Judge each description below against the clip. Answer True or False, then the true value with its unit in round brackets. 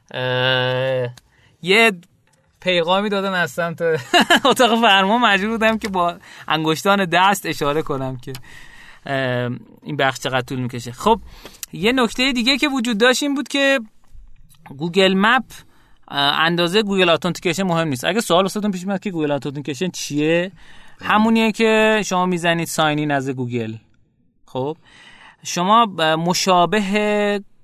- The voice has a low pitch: False (175 Hz)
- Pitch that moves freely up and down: True (6.7 semitones)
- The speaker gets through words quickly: False (125 wpm)